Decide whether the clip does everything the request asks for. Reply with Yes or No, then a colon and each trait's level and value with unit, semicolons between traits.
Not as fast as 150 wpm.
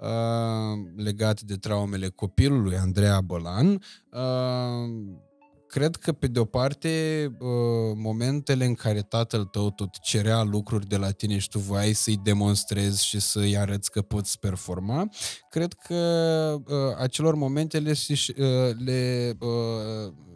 Yes: slow, 115 wpm